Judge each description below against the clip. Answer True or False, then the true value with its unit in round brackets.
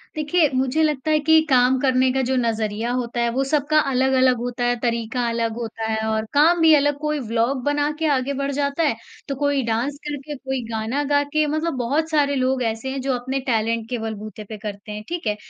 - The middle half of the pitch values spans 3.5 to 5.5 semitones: True (3.8 semitones)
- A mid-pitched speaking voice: False (260 Hz)